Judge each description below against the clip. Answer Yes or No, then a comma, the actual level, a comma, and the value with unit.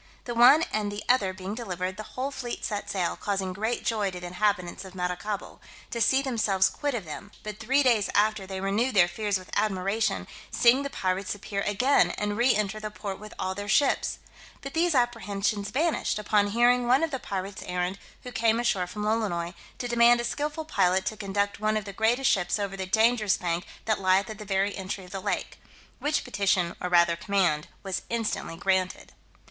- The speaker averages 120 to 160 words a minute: No, average, 200 wpm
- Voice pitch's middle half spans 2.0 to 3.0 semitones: No, average, 3.8 semitones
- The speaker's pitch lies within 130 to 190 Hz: No, high, 205 Hz